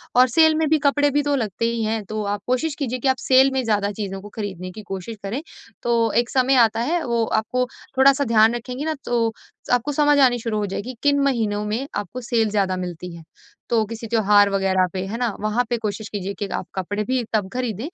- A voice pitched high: Yes, high, 230 Hz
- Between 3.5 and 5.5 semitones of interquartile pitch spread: Yes, average, 3.9 semitones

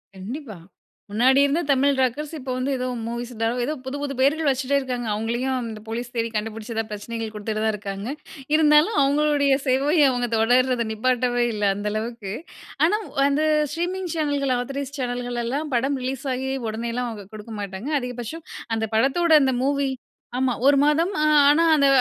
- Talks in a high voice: Yes, very high, 255 Hz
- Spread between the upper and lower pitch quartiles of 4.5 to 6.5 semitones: No, average, 3.7 semitones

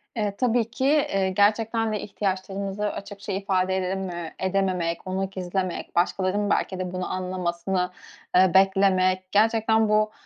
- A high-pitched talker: Yes, high, 195 Hz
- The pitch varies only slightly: Yes, narrow, 2.0 semitones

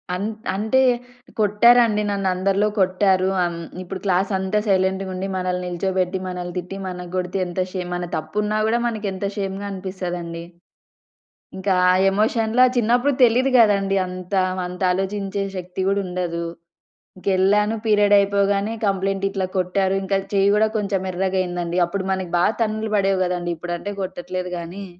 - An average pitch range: No, narrow, 2.0 semitones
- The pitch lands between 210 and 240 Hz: No, high, 195 Hz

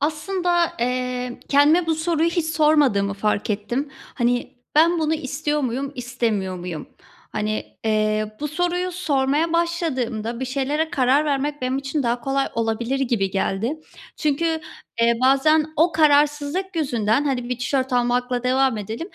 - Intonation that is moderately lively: Yes, average, 4.6 semitones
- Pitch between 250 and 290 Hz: Yes, very high, 270 Hz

